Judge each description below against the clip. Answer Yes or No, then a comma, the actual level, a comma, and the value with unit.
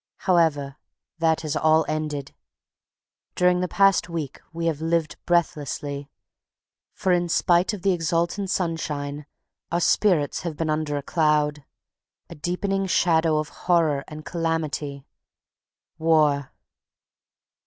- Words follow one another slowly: Yes, slow, 120 wpm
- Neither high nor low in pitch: Yes, medium, 160 Hz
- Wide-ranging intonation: No, average, 2.7 semitones